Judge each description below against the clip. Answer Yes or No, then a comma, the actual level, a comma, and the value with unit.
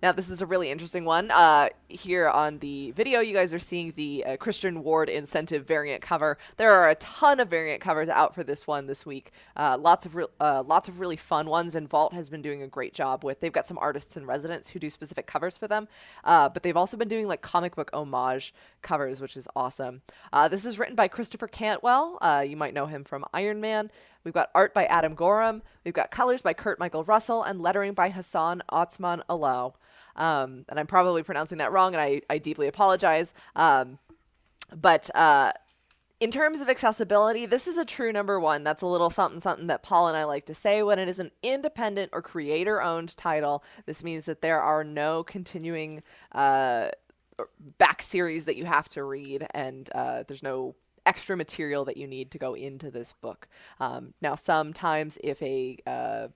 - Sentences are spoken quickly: Yes, fast, 210 wpm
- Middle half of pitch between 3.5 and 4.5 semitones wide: No, average, 5.0 semitones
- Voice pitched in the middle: Yes, medium, 165 Hz